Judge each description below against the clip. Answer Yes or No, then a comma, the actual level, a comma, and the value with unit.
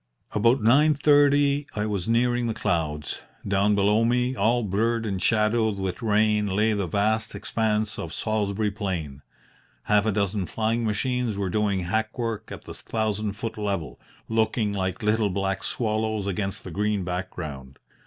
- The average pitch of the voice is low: Yes, low, 105 Hz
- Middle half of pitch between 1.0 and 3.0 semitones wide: Yes, narrow, 2.5 semitones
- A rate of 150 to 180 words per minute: Yes, average, 155 wpm